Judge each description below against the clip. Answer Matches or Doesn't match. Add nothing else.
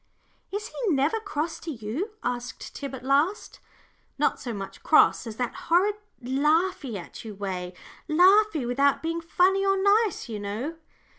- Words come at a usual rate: Matches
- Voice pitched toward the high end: Matches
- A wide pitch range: Matches